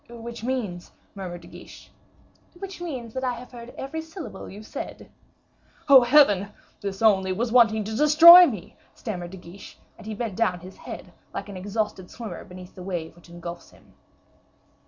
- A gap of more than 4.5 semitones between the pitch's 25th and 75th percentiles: Yes, average, 5.1 semitones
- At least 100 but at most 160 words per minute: No, average, 180 wpm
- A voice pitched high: Yes, high, 215 Hz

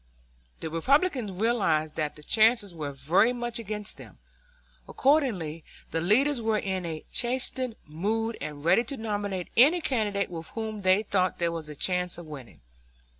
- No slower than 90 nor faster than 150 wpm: No, average, 160 wpm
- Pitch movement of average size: No, wide, 6.0 semitones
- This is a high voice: Yes, high, 200 Hz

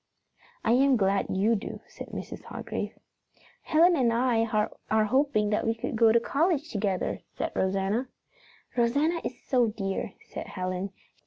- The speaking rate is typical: Yes, average, 150 wpm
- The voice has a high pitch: Yes, high, 230 Hz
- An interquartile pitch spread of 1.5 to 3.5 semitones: No, average, 4.8 semitones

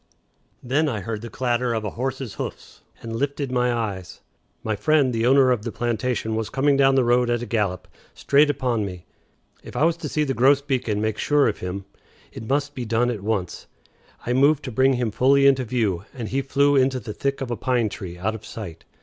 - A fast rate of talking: Yes, fast, 220 wpm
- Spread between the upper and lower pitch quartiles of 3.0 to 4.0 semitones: Yes, average, 3.6 semitones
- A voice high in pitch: No, low, 125 Hz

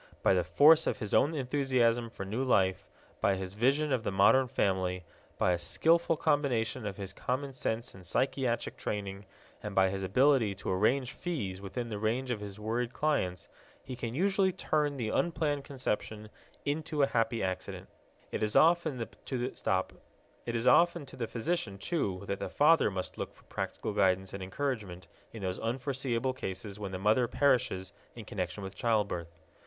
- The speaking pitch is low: Yes, low, 115 Hz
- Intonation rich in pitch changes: Yes, wide, 5.8 semitones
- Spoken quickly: No, average, 165 wpm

